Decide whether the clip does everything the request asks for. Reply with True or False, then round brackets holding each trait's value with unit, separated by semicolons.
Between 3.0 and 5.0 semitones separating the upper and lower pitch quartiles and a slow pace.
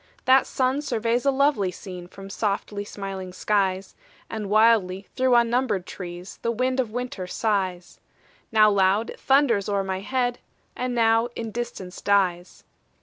False (4.1 semitones; 145 wpm)